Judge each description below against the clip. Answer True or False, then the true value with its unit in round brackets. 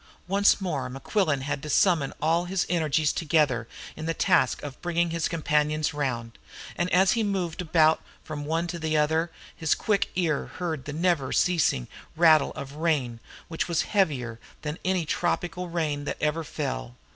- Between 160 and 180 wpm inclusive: True (170 wpm)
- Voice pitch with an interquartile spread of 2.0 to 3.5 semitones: True (3.1 semitones)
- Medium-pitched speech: True (160 Hz)